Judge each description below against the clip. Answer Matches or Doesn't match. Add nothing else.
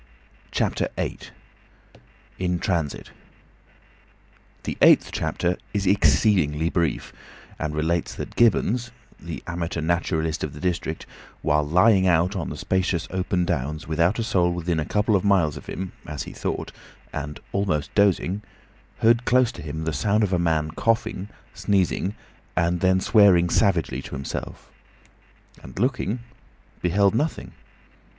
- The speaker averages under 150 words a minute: Matches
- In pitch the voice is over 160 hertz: Doesn't match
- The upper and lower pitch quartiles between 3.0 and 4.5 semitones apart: Matches